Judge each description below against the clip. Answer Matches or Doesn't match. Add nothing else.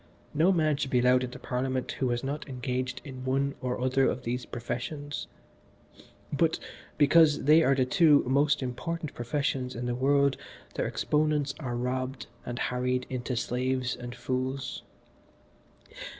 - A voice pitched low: Matches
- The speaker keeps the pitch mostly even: Matches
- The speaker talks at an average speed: Matches